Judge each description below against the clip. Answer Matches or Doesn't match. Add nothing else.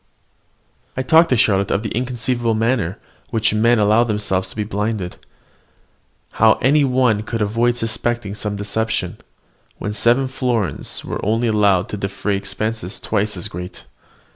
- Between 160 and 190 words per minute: Doesn't match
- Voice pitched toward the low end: Matches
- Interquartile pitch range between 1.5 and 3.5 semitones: Matches